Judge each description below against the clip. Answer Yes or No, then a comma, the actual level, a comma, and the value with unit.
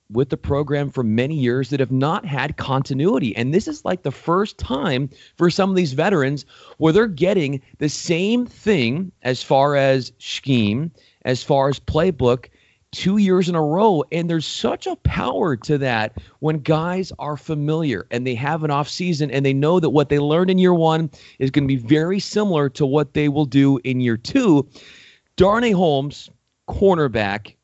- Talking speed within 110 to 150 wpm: No, average, 185 wpm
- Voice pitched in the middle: Yes, medium, 150 Hz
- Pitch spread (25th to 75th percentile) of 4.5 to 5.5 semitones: Yes, average, 4.8 semitones